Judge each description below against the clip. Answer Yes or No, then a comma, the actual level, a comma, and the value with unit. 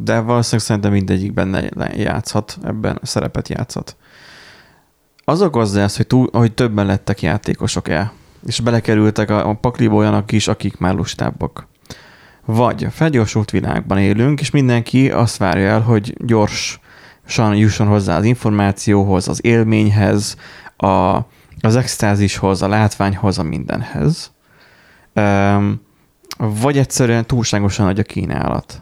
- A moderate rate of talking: Yes, average, 125 wpm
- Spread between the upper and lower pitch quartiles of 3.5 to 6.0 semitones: No, narrow, 2.6 semitones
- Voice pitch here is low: Yes, low, 105 Hz